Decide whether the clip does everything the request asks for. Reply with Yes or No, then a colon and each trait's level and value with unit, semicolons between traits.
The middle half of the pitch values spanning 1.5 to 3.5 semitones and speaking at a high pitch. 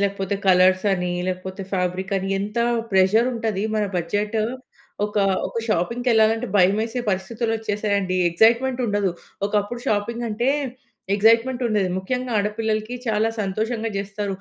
Yes: average, 2.8 semitones; high, 210 Hz